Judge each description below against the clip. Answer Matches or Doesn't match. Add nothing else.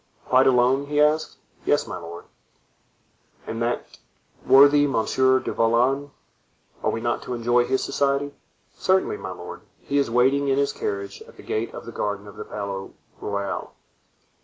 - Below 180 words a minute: Matches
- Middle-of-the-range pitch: Doesn't match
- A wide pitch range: Doesn't match